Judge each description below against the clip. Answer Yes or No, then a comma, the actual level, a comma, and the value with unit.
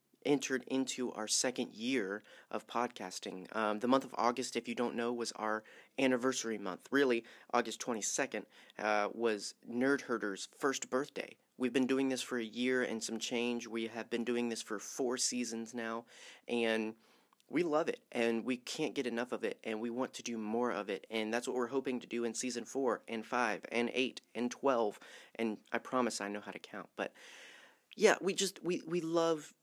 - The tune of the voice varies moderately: No, narrow, 2.3 semitones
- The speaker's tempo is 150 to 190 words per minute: No, average, 200 wpm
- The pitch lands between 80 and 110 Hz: No, low, 120 Hz